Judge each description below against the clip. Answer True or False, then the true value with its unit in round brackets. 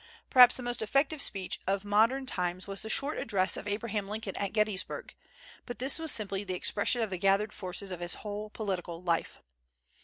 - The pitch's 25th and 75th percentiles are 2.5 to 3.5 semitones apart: True (3.0 semitones)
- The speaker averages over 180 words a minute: True (190 wpm)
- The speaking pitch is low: False (205 Hz)